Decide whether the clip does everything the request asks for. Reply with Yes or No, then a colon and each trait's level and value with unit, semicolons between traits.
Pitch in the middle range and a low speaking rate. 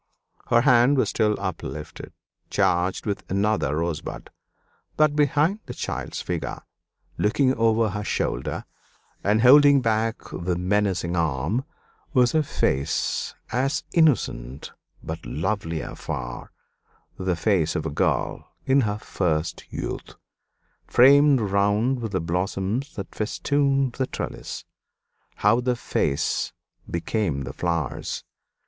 No: low, 105 Hz; slow, 115 wpm